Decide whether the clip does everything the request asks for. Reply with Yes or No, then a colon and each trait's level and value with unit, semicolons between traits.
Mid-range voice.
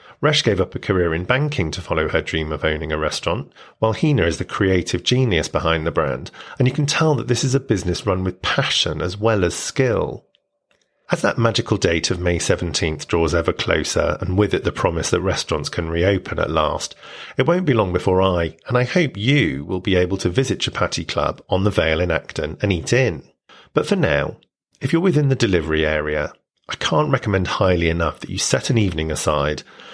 No: very low, 95 Hz